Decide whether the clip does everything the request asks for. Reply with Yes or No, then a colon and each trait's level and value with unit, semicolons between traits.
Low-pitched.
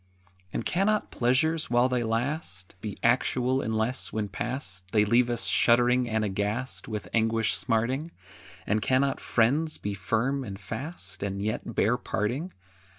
Yes: low, 115 Hz